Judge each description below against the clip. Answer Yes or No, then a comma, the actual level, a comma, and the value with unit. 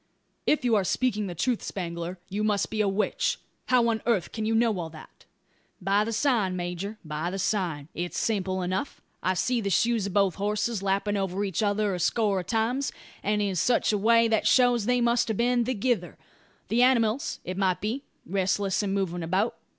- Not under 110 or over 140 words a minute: No, average, 200 wpm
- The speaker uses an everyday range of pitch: Yes, average, 3.6 semitones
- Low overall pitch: No, high, 205 Hz